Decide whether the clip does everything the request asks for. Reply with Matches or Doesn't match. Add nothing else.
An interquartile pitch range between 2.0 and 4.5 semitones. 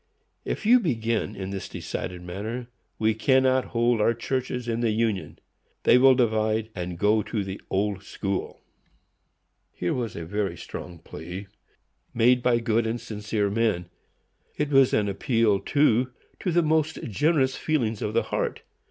Matches